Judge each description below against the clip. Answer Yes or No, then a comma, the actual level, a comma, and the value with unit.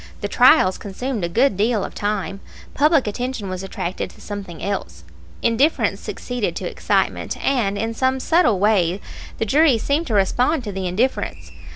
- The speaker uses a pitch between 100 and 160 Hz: No, high, 215 Hz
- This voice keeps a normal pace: Yes, average, 165 wpm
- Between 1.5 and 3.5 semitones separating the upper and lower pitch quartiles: No, average, 4.9 semitones